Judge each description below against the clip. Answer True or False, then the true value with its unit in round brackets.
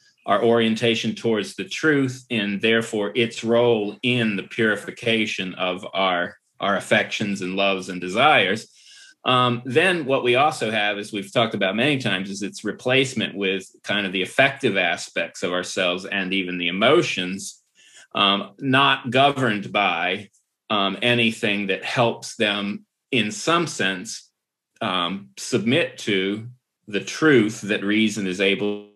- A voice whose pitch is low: True (105 Hz)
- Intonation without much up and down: False (3.6 semitones)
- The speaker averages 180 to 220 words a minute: False (140 wpm)